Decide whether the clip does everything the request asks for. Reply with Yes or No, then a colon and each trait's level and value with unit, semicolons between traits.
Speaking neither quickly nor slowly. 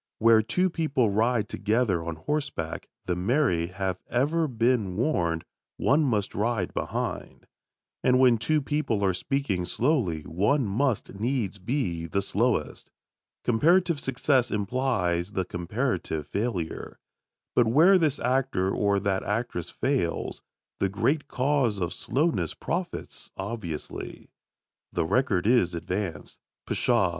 No: slow, 125 wpm